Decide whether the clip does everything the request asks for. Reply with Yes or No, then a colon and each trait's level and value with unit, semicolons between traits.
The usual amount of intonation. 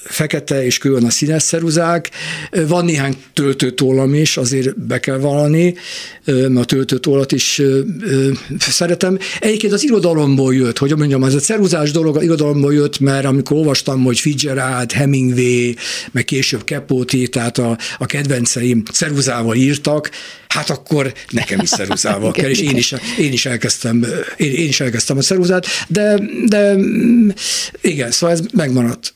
Yes: average, 4.5 semitones